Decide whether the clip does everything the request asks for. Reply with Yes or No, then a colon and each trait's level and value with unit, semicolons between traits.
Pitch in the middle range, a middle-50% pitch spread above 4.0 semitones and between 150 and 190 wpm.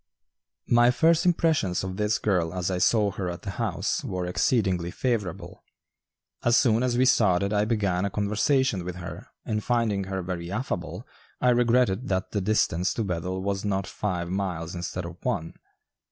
No: low, 100 Hz; average, 4.4 semitones; average, 170 wpm